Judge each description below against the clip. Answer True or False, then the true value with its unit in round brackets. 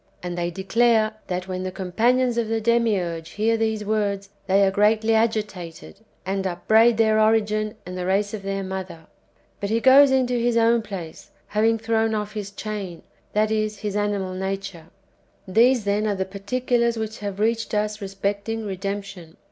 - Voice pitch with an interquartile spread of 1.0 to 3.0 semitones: True (2.6 semitones)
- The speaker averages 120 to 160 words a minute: False (170 wpm)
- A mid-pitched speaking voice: False (210 Hz)